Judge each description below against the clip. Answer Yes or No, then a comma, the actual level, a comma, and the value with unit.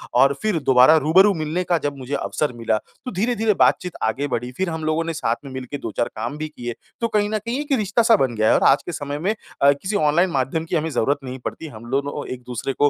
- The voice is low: No, medium, 150 Hz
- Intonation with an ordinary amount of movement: No, wide, 6.0 semitones